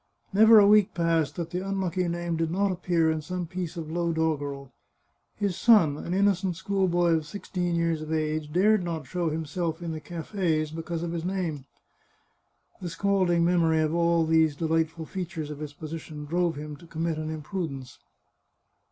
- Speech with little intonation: Yes, narrow, 2.3 semitones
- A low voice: No, medium, 165 Hz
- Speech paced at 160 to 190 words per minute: Yes, average, 180 wpm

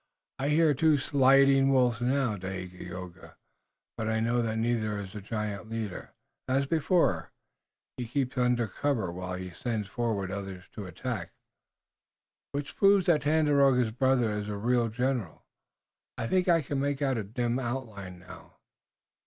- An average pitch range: Yes, average, 4.8 semitones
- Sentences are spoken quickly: No, average, 155 wpm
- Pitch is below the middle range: Yes, low, 120 Hz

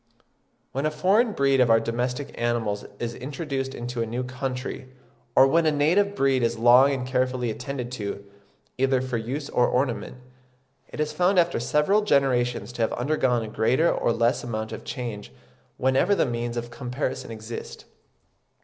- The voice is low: Yes, low, 125 Hz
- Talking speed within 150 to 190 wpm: Yes, average, 165 wpm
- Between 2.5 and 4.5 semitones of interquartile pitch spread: Yes, average, 2.9 semitones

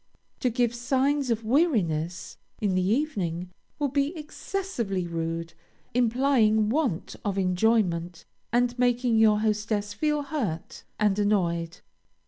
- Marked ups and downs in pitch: Yes, wide, 5.8 semitones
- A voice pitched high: Yes, high, 220 Hz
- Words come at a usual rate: No, slow, 115 wpm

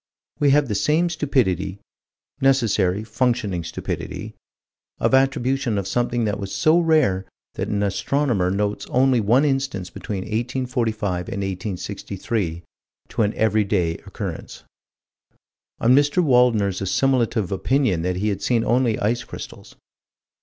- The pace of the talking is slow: Yes, slow, 130 wpm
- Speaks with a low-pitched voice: Yes, low, 110 Hz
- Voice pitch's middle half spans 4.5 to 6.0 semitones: Yes, average, 5.1 semitones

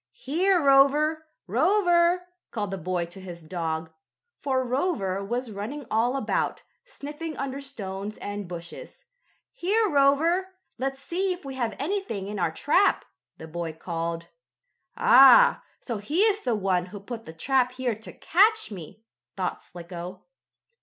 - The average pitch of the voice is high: Yes, very high, 250 Hz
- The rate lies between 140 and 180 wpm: Yes, average, 145 wpm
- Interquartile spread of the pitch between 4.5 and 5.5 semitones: No, wide, 8.8 semitones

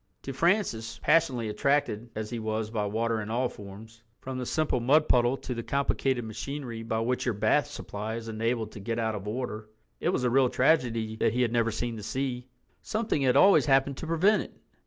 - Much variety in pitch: No, average, 3.4 semitones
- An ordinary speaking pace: No, fast, 210 wpm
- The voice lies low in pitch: Yes, low, 120 Hz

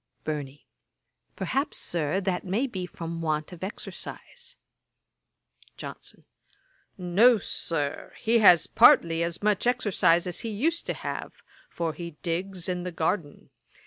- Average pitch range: Yes, average, 4.0 semitones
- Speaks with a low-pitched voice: No, medium, 180 Hz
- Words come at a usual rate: No, slow, 130 wpm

